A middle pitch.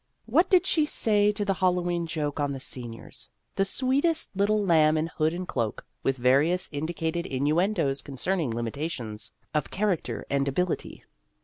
Yes: medium, 165 Hz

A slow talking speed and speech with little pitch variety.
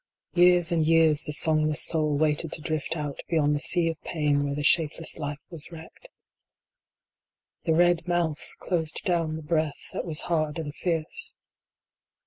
No: average, 160 wpm; narrow, 1.9 semitones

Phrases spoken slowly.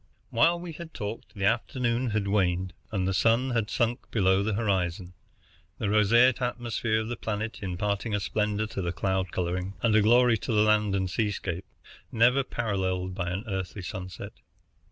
No: average, 175 wpm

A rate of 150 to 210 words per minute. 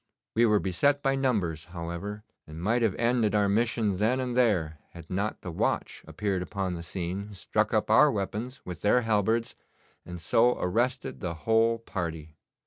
Yes: average, 170 wpm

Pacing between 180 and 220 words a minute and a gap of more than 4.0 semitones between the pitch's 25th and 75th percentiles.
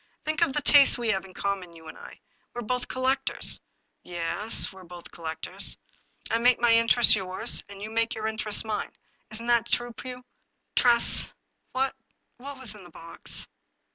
Yes: average, 200 wpm; average, 4.5 semitones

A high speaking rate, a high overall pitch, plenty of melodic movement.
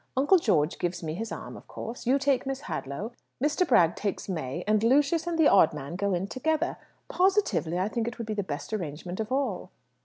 Yes: fast, 215 wpm; high, 220 Hz; wide, 7.9 semitones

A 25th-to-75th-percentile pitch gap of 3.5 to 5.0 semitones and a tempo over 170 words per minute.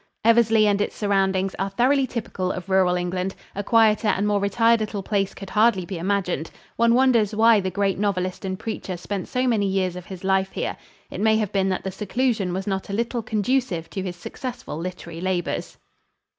No: average, 2.9 semitones; average, 200 wpm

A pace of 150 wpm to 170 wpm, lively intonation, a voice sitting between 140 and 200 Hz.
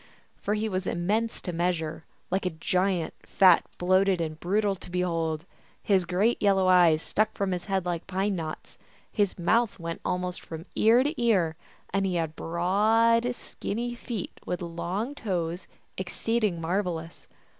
No: average, 155 wpm; average, 3.4 semitones; medium, 185 Hz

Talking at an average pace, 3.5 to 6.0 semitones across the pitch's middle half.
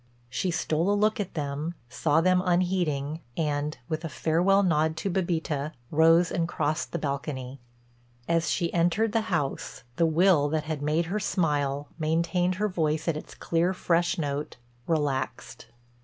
No: average, 155 wpm; average, 2.9 semitones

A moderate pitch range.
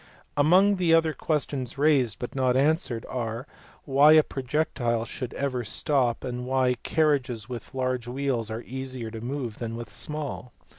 Yes: average, 3.3 semitones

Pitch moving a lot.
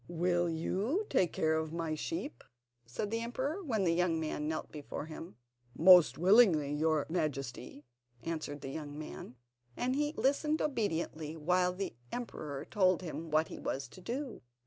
Yes: wide, 6.1 semitones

